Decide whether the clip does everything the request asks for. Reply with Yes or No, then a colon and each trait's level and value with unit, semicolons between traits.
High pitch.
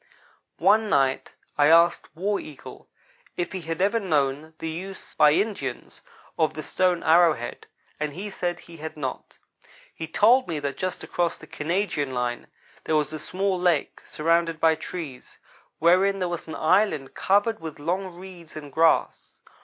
No: medium, 165 Hz